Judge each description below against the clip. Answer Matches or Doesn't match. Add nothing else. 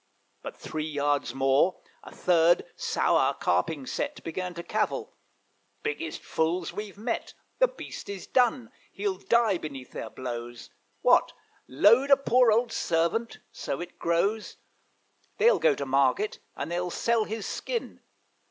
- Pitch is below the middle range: Doesn't match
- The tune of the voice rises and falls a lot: Matches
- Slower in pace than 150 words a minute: Matches